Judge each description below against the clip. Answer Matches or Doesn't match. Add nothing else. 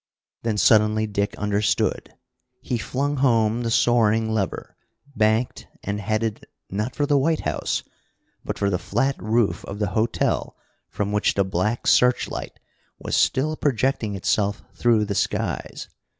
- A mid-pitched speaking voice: Doesn't match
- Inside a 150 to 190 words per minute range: Doesn't match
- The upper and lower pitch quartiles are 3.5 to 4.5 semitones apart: Doesn't match